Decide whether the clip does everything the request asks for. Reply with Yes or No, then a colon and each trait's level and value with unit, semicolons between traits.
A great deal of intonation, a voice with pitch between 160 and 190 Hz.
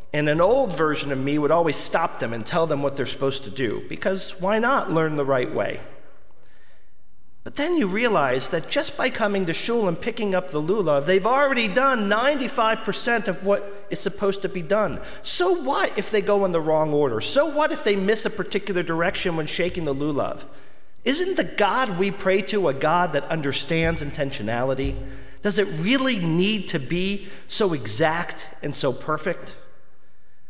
Yes: wide, 5.8 semitones; medium, 185 Hz